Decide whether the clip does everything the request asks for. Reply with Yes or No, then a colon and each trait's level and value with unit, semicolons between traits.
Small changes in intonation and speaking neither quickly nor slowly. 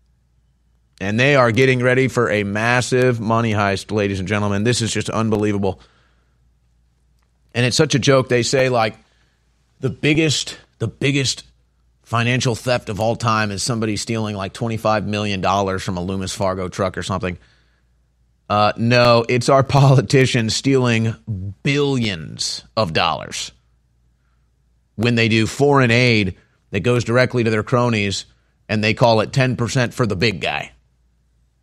No: wide, 5.4 semitones; average, 150 wpm